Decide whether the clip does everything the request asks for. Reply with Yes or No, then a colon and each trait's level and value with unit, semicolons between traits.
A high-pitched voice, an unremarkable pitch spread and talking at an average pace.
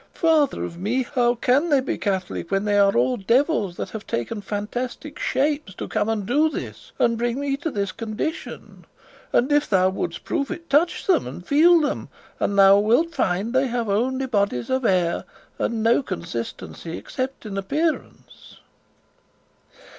No: high, 230 Hz; wide, 6.1 semitones; average, 170 wpm